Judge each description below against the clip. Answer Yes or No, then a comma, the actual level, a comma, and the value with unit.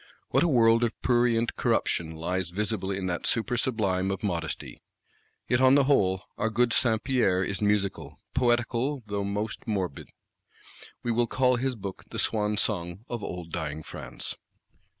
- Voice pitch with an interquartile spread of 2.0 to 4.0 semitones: No, average, 4.5 semitones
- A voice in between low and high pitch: No, low, 105 Hz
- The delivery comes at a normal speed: Yes, average, 160 wpm